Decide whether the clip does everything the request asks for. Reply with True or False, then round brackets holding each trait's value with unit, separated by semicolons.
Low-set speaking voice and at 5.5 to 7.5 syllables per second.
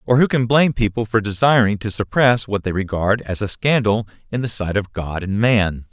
False (110 Hz; 5.2 syllables/s)